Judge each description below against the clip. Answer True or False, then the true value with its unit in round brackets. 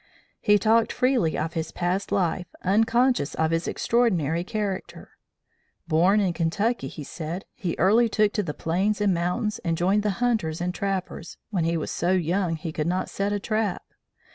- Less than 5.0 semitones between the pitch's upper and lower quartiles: True (4.1 semitones)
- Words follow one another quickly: False (175 wpm)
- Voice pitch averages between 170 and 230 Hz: True (185 Hz)